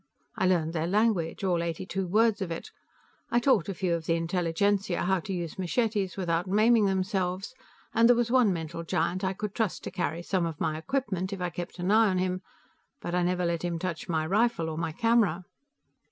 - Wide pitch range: No, average, 3.2 semitones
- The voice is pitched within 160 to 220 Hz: Yes, medium, 185 Hz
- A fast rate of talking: Yes, fast, 210 wpm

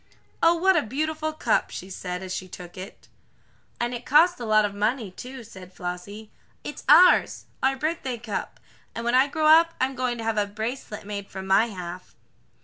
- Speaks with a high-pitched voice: Yes, high, 230 Hz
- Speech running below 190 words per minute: No, average, 195 wpm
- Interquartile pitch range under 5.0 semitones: No, wide, 5.5 semitones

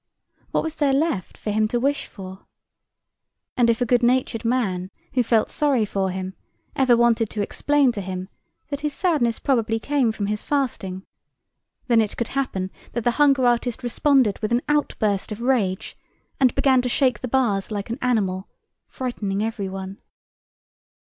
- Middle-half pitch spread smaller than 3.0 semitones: No, average, 4.4 semitones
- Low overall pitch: No, high, 235 Hz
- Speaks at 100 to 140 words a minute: No, average, 170 wpm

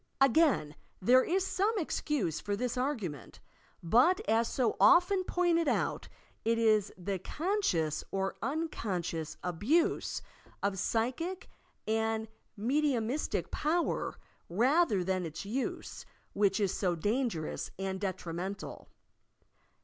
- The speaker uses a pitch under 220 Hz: No, high, 225 Hz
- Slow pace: Yes, slow, 110 wpm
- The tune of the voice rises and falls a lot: Yes, wide, 8.0 semitones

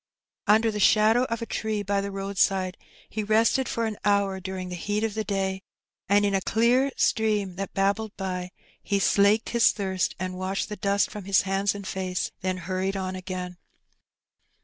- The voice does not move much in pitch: Yes, narrow, 2.1 semitones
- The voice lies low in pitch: No, high, 200 Hz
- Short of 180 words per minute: No, average, 185 wpm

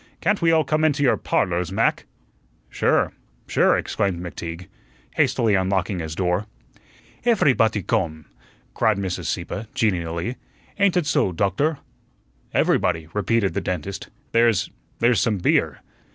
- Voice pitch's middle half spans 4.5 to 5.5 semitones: Yes, average, 5.1 semitones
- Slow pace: Yes, slow, 130 wpm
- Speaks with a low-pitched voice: Yes, low, 100 Hz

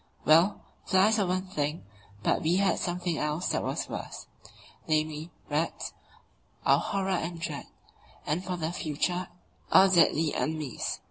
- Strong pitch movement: No, average, 3.0 semitones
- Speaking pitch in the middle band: Yes, medium, 170 Hz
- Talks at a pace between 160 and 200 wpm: No, average, 140 wpm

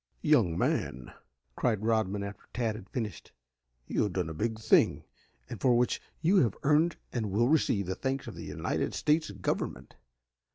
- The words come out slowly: No, average, 170 wpm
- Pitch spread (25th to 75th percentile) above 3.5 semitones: Yes, average, 4.5 semitones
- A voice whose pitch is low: Yes, low, 110 Hz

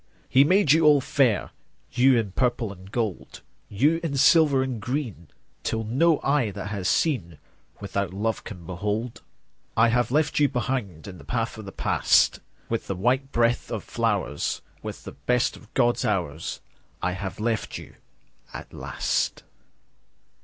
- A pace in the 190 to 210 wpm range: No, average, 165 wpm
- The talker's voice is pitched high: No, low, 115 Hz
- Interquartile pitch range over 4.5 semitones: Yes, average, 5.1 semitones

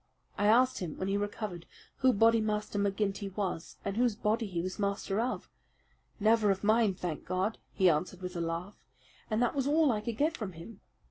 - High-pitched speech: Yes, high, 205 Hz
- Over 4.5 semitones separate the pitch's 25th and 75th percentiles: No, average, 3.4 semitones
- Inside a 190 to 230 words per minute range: Yes, average, 195 wpm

